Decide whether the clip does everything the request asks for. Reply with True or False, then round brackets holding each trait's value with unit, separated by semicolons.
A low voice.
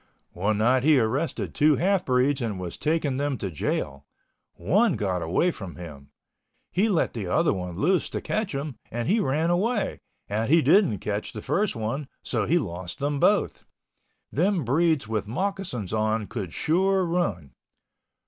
True (130 Hz)